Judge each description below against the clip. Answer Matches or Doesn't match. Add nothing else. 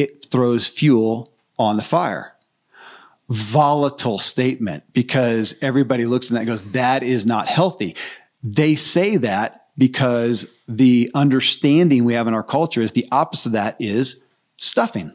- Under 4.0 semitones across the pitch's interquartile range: Matches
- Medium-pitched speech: Doesn't match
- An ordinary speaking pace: Matches